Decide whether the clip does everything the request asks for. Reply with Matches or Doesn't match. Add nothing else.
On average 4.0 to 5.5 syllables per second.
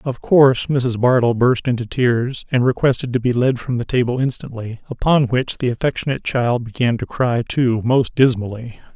Matches